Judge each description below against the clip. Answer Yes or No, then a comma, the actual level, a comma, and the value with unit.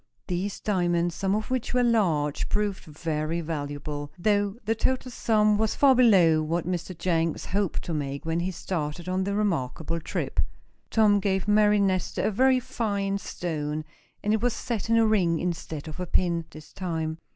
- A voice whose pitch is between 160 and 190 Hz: Yes, medium, 185 Hz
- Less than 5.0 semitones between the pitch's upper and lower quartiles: Yes, average, 4.4 semitones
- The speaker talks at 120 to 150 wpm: No, average, 175 wpm